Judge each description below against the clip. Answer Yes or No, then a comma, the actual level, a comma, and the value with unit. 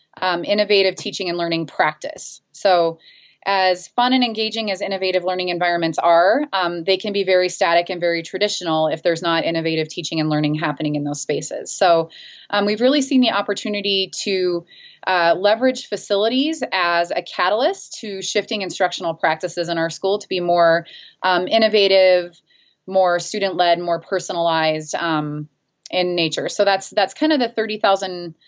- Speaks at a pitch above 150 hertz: Yes, medium, 185 Hz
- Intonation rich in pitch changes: No, average, 3.3 semitones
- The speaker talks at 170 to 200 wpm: No, average, 160 wpm